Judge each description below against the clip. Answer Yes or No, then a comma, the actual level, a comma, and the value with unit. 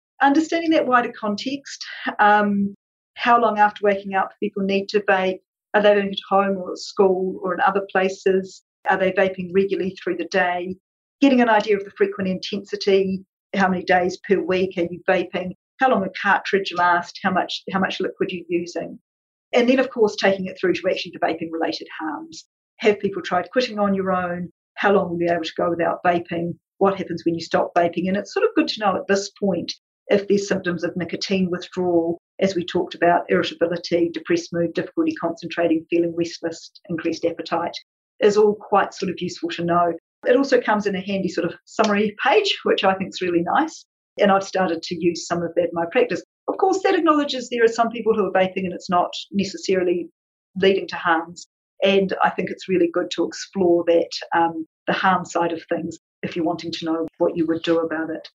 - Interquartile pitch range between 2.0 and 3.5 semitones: Yes, average, 2.7 semitones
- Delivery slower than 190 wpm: No, fast, 205 wpm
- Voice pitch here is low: No, medium, 185 Hz